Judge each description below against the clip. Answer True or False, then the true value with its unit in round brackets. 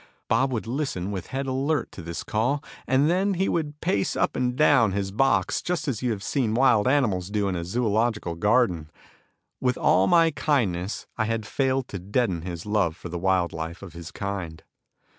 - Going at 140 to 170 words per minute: False (195 wpm)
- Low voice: True (110 Hz)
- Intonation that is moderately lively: False (6.2 semitones)